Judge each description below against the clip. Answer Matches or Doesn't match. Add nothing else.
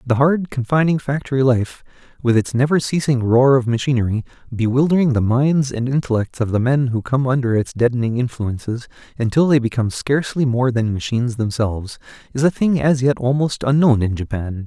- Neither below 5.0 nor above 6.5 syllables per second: Matches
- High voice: Doesn't match